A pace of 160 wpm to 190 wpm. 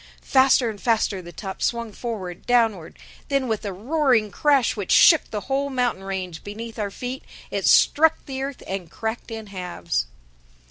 Yes: average, 170 wpm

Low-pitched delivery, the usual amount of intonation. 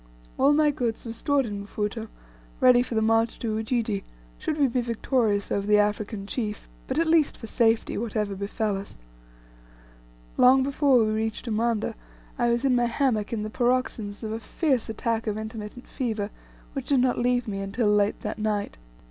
No: high, 225 Hz; average, 3.0 semitones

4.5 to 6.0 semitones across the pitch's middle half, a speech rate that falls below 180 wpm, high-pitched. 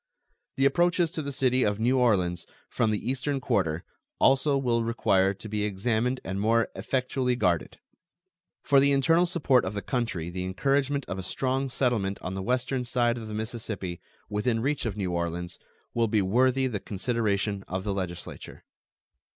No: average, 5.1 semitones; average, 170 wpm; low, 115 Hz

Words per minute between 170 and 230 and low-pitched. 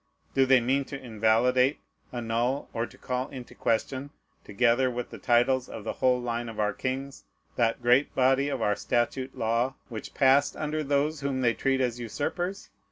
Yes: average, 175 wpm; low, 125 Hz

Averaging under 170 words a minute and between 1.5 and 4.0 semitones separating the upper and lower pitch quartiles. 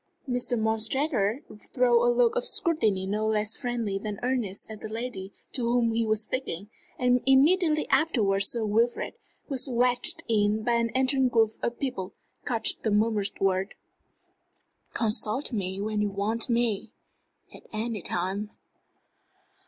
Yes: average, 145 wpm; average, 3.0 semitones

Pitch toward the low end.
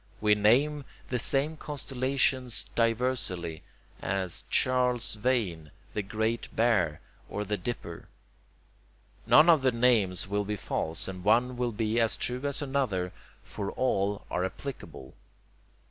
Yes: low, 115 Hz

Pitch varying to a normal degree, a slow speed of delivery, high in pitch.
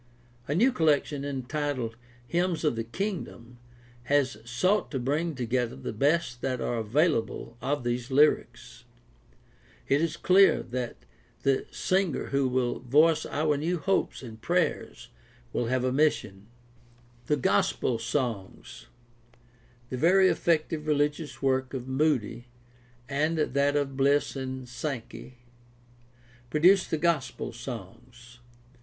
No: average, 4.1 semitones; slow, 125 wpm; low, 135 Hz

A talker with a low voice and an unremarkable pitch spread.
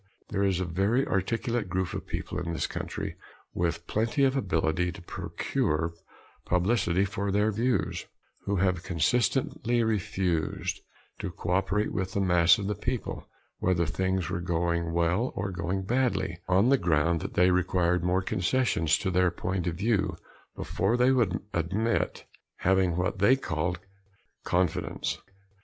Yes: very low, 95 Hz; average, 3.1 semitones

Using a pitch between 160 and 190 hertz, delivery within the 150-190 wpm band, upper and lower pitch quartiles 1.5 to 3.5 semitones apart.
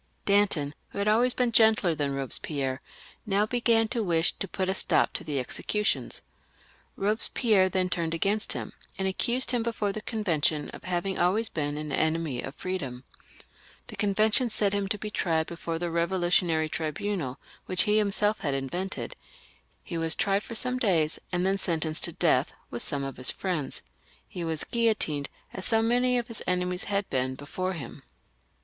No: medium, 185 Hz; average, 175 wpm; average, 5.0 semitones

